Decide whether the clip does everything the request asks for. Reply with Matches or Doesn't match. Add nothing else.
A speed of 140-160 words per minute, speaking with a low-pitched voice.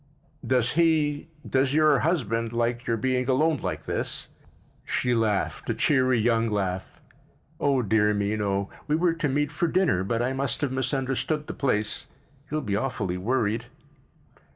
Matches